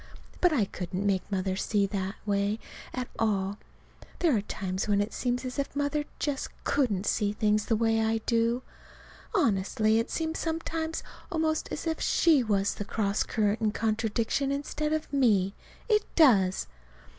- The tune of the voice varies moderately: No, wide, 5.8 semitones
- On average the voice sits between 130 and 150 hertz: No, high, 225 Hz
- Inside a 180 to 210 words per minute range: No, average, 165 wpm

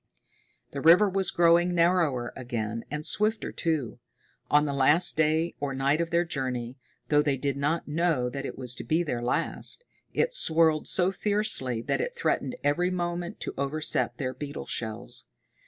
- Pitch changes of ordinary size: Yes, average, 4.5 semitones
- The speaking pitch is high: No, medium, 155 Hz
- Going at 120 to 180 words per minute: Yes, average, 170 wpm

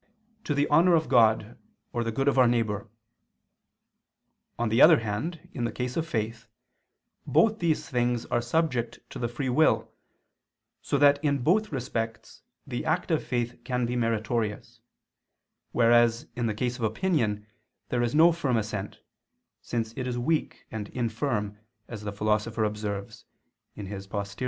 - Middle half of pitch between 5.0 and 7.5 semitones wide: No, average, 4.1 semitones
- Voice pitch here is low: Yes, low, 120 Hz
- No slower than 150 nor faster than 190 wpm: Yes, average, 155 wpm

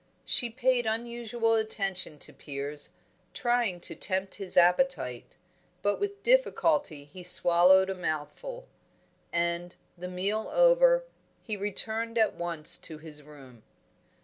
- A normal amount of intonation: No, wide, 5.8 semitones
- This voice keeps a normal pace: No, slow, 120 wpm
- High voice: Yes, high, 195 Hz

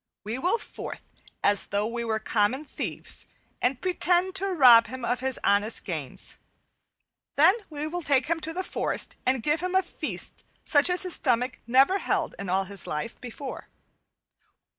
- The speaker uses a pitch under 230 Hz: No, very high, 260 Hz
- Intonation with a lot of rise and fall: Yes, wide, 7.0 semitones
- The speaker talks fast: No, average, 170 wpm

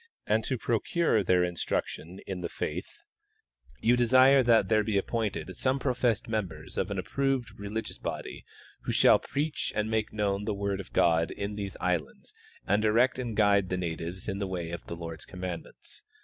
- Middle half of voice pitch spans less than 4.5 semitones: Yes, average, 4.0 semitones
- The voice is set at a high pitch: No, low, 100 Hz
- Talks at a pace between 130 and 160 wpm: No, average, 175 wpm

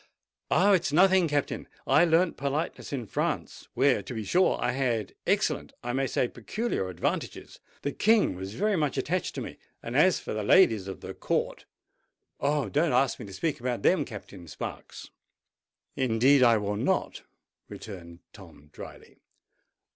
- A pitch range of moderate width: No, wide, 7.0 semitones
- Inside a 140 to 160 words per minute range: Yes, average, 155 wpm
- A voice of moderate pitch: No, low, 130 Hz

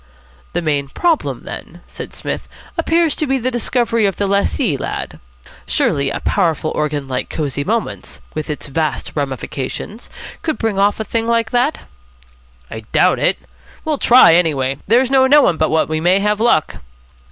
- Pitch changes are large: Yes, wide, 8.0 semitones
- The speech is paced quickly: No, average, 165 wpm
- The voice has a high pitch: Yes, high, 200 Hz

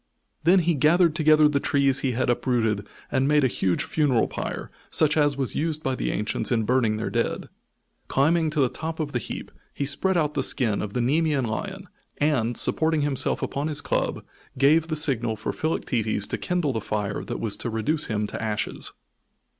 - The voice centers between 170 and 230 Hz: No, medium, 140 Hz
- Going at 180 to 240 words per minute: Yes, average, 195 wpm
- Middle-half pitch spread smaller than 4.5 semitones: No, average, 5.1 semitones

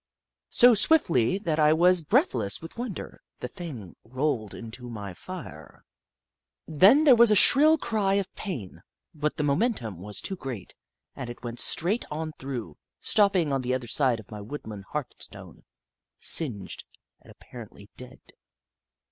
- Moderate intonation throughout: No, wide, 8.4 semitones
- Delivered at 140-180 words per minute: Yes, average, 150 wpm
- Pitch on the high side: No, medium, 145 Hz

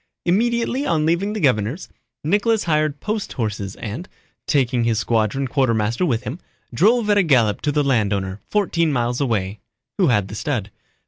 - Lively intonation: Yes, wide, 7.9 semitones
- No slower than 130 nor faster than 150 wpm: No, average, 165 wpm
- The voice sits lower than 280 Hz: Yes, low, 135 Hz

